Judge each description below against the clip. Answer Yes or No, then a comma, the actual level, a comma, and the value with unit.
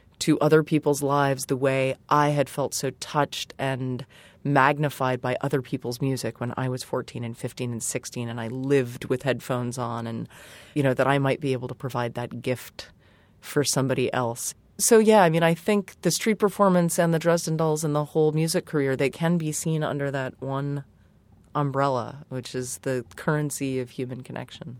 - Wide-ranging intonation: No, average, 2.9 semitones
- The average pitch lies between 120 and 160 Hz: Yes, low, 135 Hz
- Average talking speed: Yes, average, 190 wpm